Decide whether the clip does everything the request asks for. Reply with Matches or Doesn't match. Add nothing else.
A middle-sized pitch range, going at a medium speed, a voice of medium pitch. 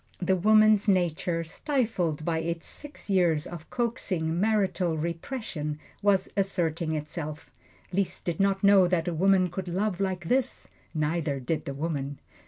Matches